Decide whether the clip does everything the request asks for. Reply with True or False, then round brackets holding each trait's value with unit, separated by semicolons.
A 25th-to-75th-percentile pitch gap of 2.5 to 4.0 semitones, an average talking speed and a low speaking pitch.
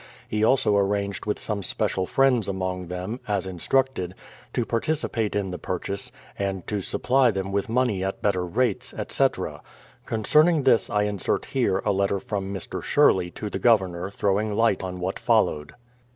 True (3.2 semitones; 165 wpm; 100 Hz)